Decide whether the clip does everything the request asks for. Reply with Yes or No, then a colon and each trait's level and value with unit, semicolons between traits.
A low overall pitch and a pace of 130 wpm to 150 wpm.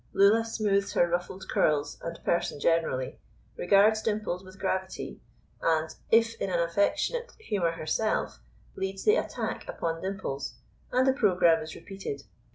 No: high, 190 Hz; average, 140 wpm